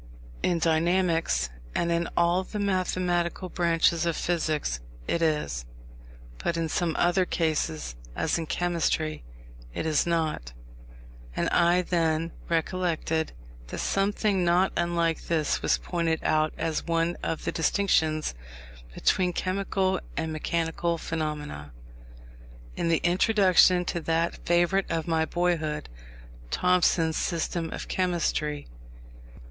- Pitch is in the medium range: Yes, medium, 170 Hz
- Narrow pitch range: Yes, narrow, 1.9 semitones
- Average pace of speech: No, slow, 120 wpm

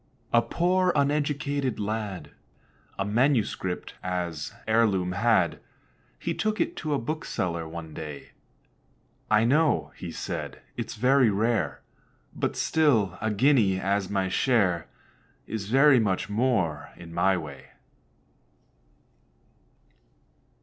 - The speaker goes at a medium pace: No, slow, 110 wpm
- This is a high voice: No, low, 105 Hz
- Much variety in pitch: Yes, wide, 6.6 semitones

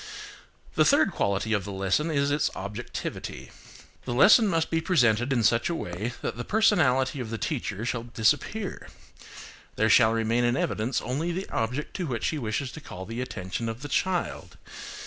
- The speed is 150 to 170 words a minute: No, average, 180 wpm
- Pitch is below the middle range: Yes, low, 120 Hz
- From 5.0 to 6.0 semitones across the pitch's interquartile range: Yes, average, 5.3 semitones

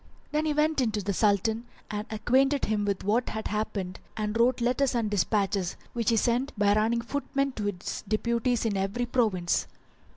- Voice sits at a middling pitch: No, high, 220 Hz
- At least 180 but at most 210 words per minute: Yes, average, 185 wpm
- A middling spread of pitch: Yes, average, 3.1 semitones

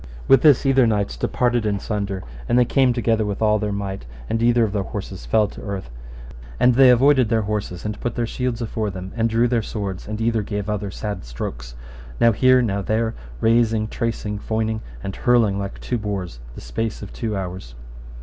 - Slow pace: No, fast, 205 wpm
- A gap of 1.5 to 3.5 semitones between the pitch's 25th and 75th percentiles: Yes, average, 2.7 semitones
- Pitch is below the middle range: Yes, low, 110 Hz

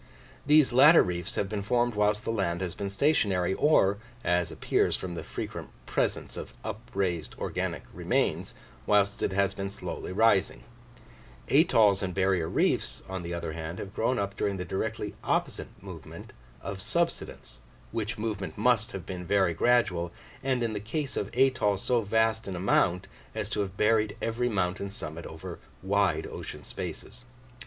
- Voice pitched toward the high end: No, low, 100 Hz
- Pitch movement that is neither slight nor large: Yes, average, 3.6 semitones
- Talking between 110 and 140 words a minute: No, average, 165 wpm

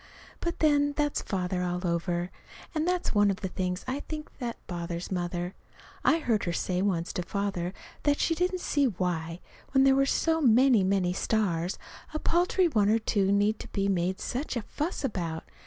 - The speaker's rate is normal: Yes, average, 190 wpm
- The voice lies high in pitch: Yes, high, 200 Hz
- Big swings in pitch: Yes, wide, 8.1 semitones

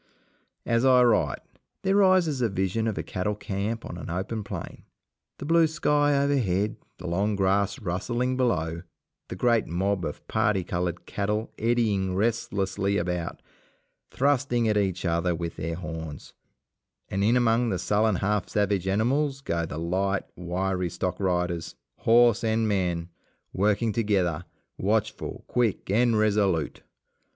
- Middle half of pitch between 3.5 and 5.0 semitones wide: Yes, average, 4.4 semitones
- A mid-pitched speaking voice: No, low, 100 Hz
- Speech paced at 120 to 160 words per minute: Yes, average, 140 wpm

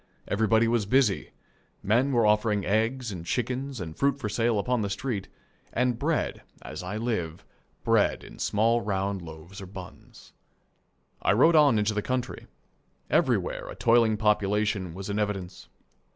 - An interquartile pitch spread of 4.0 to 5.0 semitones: No, average, 3.4 semitones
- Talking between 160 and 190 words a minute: No, average, 150 wpm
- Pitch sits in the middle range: No, low, 105 Hz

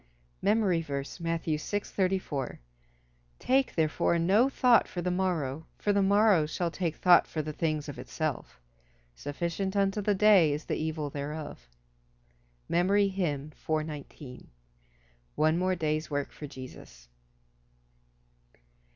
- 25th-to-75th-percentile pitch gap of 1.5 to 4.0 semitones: No, average, 4.7 semitones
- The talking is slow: Yes, slow, 125 wpm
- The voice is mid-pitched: Yes, medium, 160 Hz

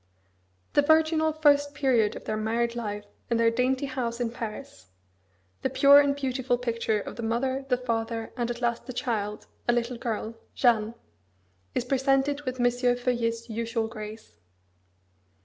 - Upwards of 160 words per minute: No, average, 155 wpm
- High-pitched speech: Yes, high, 240 Hz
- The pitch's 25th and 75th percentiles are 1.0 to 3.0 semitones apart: Yes, narrow, 2.6 semitones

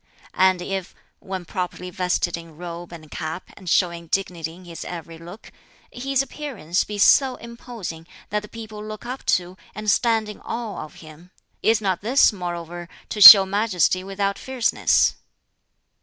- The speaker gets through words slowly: No, average, 155 wpm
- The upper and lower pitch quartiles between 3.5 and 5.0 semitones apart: Yes, average, 3.8 semitones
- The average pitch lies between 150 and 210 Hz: Yes, high, 190 Hz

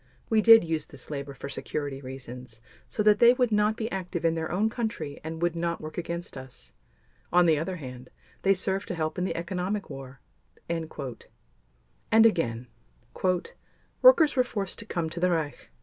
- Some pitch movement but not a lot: No, wide, 6.1 semitones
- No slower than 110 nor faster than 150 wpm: No, average, 180 wpm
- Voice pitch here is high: No, medium, 170 Hz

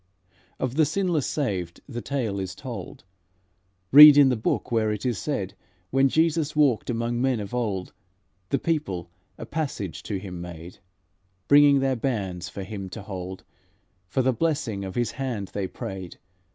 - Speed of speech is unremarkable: Yes, average, 165 wpm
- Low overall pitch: Yes, low, 120 Hz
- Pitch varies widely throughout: Yes, wide, 6.3 semitones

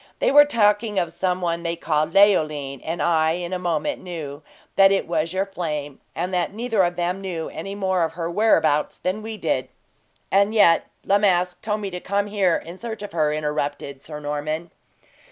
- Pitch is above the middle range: No, medium, 175 Hz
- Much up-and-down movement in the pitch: No, average, 3.8 semitones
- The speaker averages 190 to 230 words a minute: Yes, average, 195 wpm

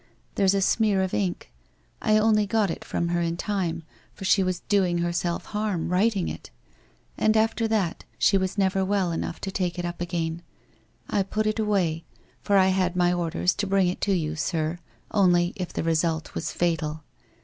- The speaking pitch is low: No, medium, 185 Hz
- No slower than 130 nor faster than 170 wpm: No, average, 190 wpm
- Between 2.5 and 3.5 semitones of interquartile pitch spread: Yes, average, 2.9 semitones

